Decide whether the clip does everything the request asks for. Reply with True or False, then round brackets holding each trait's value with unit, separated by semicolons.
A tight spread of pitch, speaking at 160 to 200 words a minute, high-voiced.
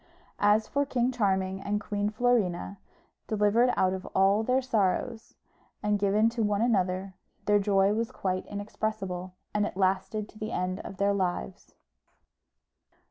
False (2.3 semitones; 145 wpm; 205 Hz)